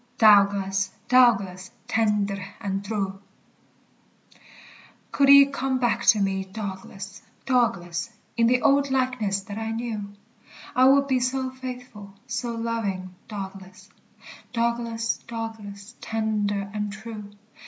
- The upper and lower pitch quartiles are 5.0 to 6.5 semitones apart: No, average, 3.5 semitones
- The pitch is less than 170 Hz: No, high, 220 Hz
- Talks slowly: Yes, slow, 110 wpm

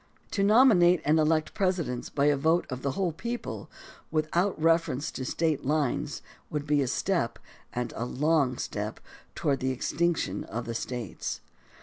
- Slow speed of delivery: No, average, 165 wpm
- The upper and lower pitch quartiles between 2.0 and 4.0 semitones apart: No, average, 4.9 semitones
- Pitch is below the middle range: No, medium, 155 Hz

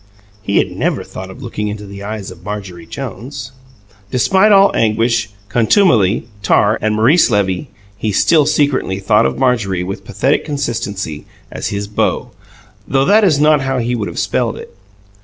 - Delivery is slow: No, average, 165 wpm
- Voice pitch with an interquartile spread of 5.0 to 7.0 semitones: Yes, wide, 5.4 semitones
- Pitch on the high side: No, low, 115 Hz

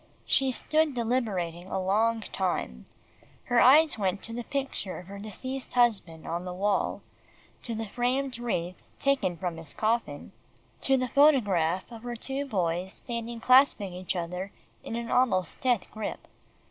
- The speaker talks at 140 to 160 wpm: Yes, average, 155 wpm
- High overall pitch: Yes, high, 220 Hz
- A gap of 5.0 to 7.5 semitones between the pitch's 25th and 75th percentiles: Yes, wide, 5.4 semitones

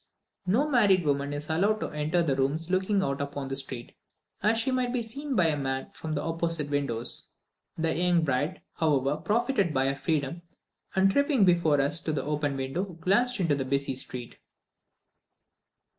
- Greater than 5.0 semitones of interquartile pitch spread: Yes, wide, 5.5 semitones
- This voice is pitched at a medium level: Yes, medium, 160 Hz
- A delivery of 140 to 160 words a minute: No, average, 175 wpm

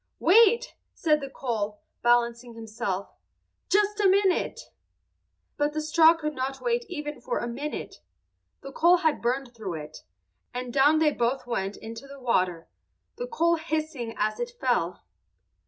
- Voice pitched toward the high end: Yes, very high, 275 Hz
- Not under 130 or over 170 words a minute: Yes, average, 150 wpm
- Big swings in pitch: Yes, wide, 5.7 semitones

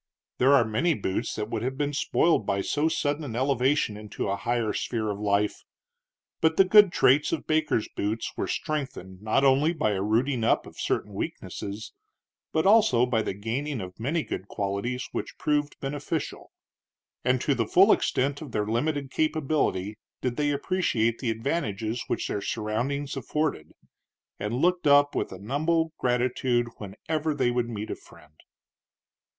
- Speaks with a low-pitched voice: Yes, low, 125 Hz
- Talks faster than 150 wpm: Yes, average, 165 wpm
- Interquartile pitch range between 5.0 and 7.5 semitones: Yes, wide, 5.4 semitones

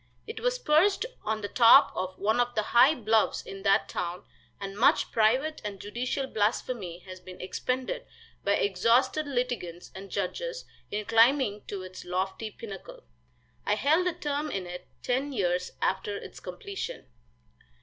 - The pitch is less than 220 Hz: No, high, 225 Hz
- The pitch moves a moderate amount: No, wide, 6.4 semitones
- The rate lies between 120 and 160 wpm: Yes, average, 155 wpm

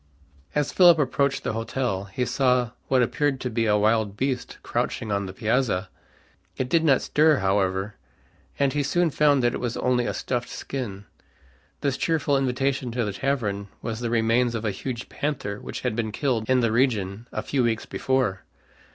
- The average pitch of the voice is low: Yes, low, 125 Hz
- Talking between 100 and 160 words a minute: No, average, 185 wpm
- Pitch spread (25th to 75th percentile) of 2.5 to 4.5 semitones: Yes, average, 4.0 semitones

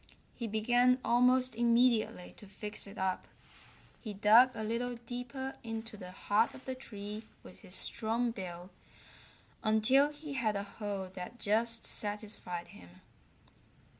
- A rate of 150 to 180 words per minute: No, slow, 135 wpm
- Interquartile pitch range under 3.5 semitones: Yes, average, 3.1 semitones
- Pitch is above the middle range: Yes, high, 225 Hz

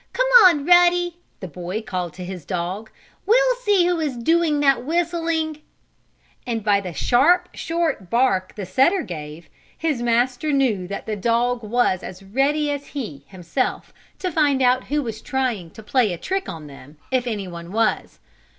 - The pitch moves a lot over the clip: Yes, wide, 8.6 semitones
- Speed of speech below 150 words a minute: No, average, 170 wpm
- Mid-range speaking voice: No, high, 245 Hz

